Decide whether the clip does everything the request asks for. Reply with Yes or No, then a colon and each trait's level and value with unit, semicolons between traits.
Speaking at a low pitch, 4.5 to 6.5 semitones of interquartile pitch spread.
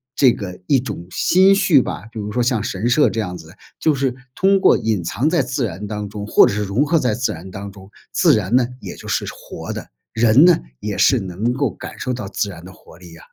Yes: low, 110 Hz; average, 4.9 semitones